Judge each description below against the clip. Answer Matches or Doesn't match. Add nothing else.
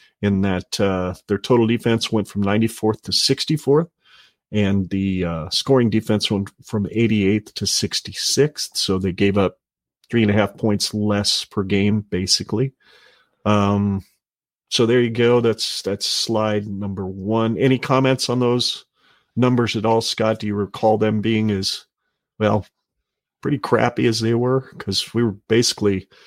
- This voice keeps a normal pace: Matches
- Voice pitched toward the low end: Matches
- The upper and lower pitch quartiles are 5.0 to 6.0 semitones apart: Doesn't match